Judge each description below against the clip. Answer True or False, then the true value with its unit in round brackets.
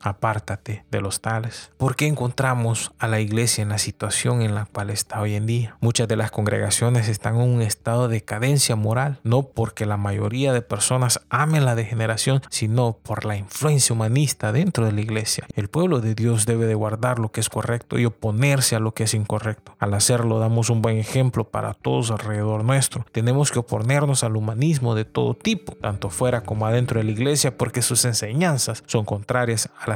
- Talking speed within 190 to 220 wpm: True (200 wpm)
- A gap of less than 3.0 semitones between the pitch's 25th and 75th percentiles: True (2.6 semitones)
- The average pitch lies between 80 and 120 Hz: True (115 Hz)